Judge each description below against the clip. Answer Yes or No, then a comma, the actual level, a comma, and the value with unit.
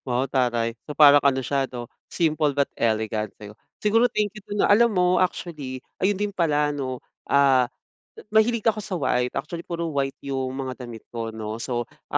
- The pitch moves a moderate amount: No, wide, 5.8 semitones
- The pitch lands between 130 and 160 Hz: Yes, medium, 140 Hz